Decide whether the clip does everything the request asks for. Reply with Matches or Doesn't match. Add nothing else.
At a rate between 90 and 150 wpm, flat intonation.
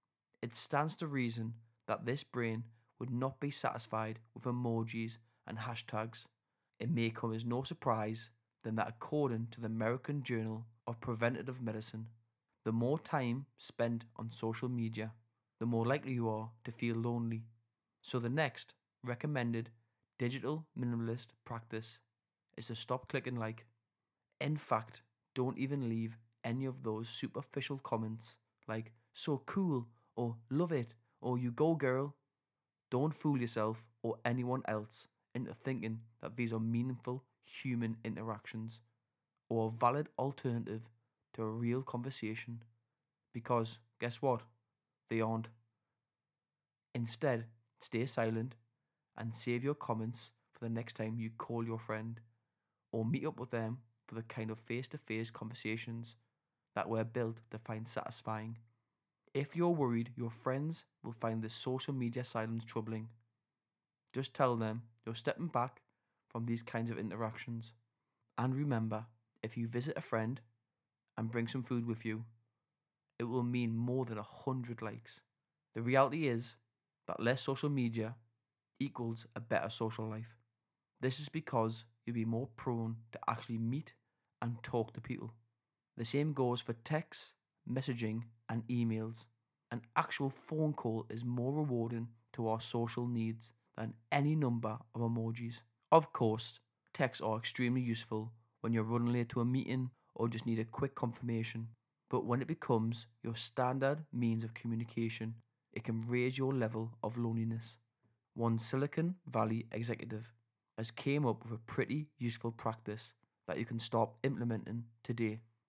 Matches